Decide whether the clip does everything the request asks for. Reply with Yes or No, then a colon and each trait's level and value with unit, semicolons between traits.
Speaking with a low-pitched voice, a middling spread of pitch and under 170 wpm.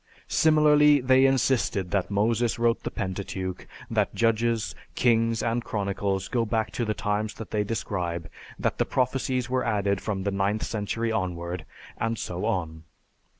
Yes: low, 110 Hz; average, 3.2 semitones; average, 150 wpm